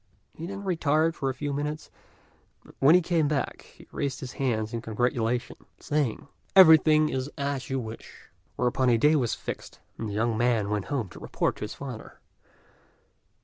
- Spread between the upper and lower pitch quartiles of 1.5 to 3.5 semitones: No, average, 4.6 semitones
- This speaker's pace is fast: No, average, 180 wpm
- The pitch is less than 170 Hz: Yes, low, 135 Hz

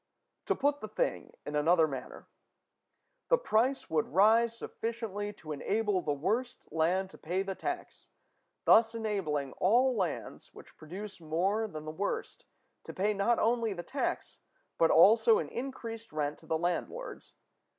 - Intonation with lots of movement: Yes, wide, 6.0 semitones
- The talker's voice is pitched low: No, high, 205 Hz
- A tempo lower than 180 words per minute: Yes, average, 150 wpm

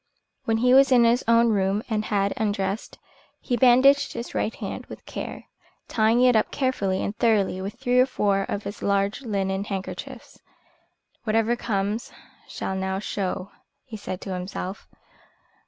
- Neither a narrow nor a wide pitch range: Yes, average, 3.4 semitones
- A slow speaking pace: No, average, 155 wpm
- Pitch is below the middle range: No, high, 215 Hz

